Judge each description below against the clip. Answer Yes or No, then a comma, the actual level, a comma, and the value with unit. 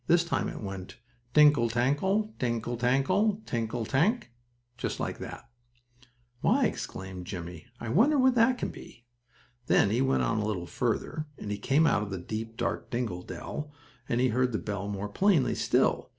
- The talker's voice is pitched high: No, low, 120 Hz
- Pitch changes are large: Yes, wide, 6.5 semitones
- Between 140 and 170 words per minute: No, average, 180 wpm